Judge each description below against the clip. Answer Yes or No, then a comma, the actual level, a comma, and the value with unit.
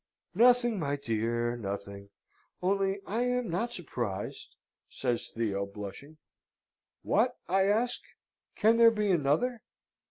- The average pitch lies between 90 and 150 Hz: No, medium, 170 Hz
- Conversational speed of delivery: No, slow, 115 wpm